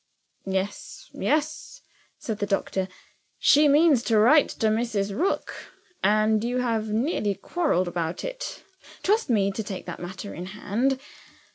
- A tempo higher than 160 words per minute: No, average, 140 wpm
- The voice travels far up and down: Yes, wide, 6.2 semitones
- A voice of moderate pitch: No, high, 220 Hz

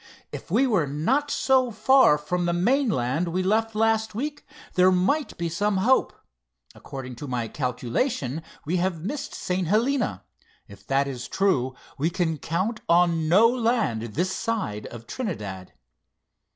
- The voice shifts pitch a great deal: Yes, wide, 7.9 semitones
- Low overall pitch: No, medium, 180 Hz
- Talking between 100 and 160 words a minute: Yes, average, 150 wpm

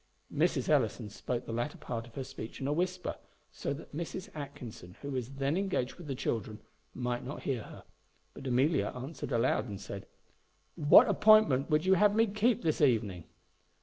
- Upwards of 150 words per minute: Yes, average, 180 wpm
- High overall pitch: No, low, 135 Hz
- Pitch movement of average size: No, wide, 6.0 semitones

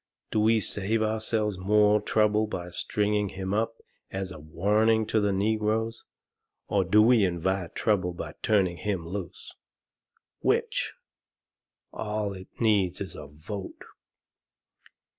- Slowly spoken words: Yes, slow, 125 wpm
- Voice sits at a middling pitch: No, low, 105 Hz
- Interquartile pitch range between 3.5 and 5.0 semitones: No, narrow, 2.5 semitones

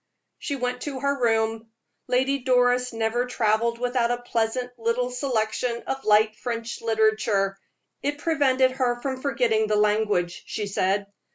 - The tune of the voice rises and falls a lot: No, narrow, 2.5 semitones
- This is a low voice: No, high, 240 Hz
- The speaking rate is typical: Yes, average, 145 wpm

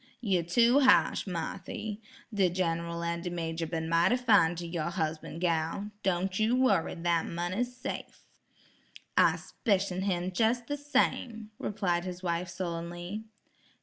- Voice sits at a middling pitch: Yes, medium, 180 Hz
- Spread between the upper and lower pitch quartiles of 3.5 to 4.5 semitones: Yes, average, 4.1 semitones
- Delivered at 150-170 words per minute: No, average, 140 wpm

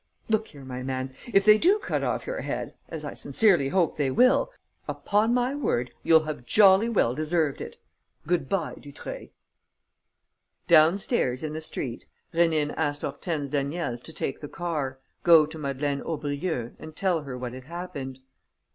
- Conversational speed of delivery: Yes, average, 165 wpm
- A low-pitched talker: No, medium, 155 Hz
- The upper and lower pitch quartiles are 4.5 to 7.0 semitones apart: Yes, average, 4.8 semitones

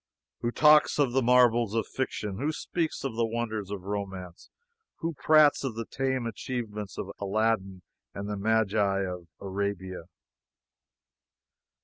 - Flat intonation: No, average, 4.2 semitones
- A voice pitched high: No, low, 110 Hz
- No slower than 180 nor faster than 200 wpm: No, slow, 135 wpm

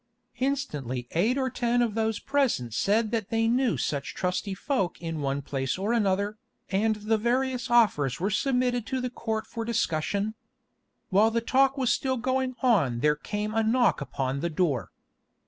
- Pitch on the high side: Yes, high, 220 Hz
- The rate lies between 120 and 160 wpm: No, average, 170 wpm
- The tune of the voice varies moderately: No, wide, 6.1 semitones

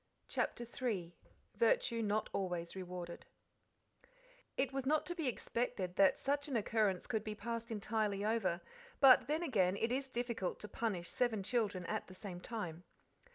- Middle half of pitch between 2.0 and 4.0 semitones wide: No, average, 4.9 semitones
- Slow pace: No, average, 155 wpm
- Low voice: No, high, 220 Hz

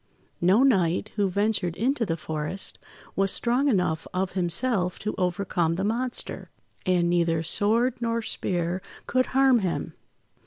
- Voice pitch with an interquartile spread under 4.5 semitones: No, average, 4.9 semitones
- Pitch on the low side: No, high, 195 Hz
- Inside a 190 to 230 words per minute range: No, average, 140 wpm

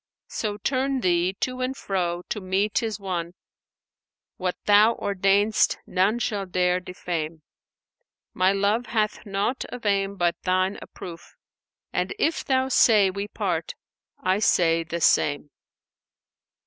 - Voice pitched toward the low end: No, high, 195 Hz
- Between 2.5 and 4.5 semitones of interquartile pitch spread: Yes, average, 3.0 semitones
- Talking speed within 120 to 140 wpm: Yes, slow, 135 wpm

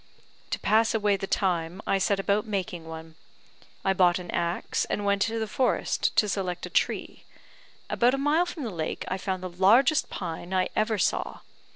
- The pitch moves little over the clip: No, average, 3.5 semitones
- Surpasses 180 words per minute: Yes, average, 190 wpm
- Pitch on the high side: Yes, high, 195 Hz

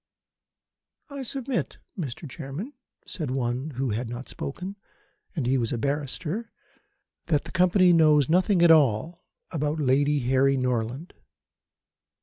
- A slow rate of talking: Yes, slow, 130 wpm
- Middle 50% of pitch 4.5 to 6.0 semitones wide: Yes, average, 5.1 semitones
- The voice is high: No, medium, 145 Hz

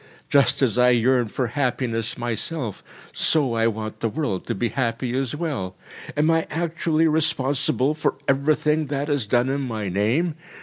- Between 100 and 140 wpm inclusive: No, average, 165 wpm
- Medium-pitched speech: No, low, 130 Hz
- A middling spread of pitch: Yes, average, 4.7 semitones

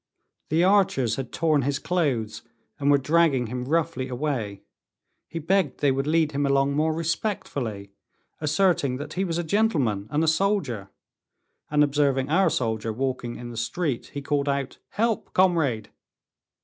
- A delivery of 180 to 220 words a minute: No, average, 155 wpm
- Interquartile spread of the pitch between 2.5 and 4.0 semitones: No, average, 4.6 semitones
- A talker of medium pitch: Yes, medium, 145 Hz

